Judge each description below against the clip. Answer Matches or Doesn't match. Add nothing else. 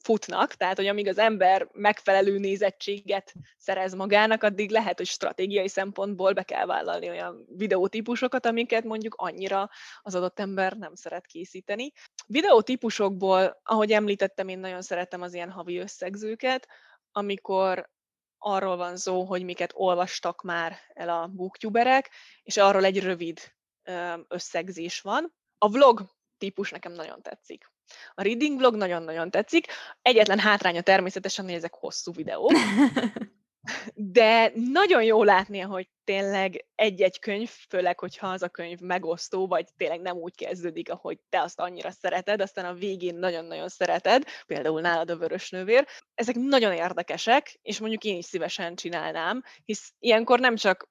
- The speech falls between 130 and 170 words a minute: Matches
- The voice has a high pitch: Matches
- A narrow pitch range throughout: Doesn't match